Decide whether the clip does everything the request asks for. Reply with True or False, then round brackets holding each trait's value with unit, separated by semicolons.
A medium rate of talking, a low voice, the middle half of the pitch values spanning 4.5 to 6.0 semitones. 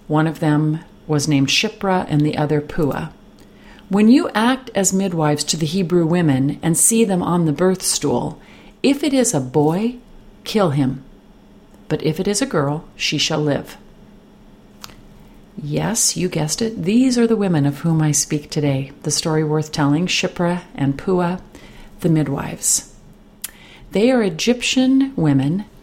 False (160 wpm; 165 Hz; 5.3 semitones)